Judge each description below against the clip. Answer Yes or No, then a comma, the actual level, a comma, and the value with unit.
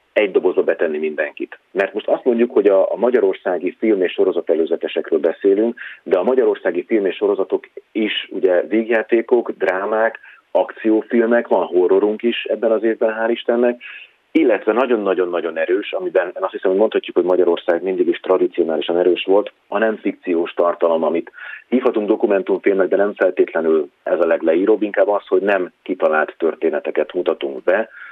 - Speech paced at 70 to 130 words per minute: No, fast, 155 wpm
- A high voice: Yes, very high, 385 Hz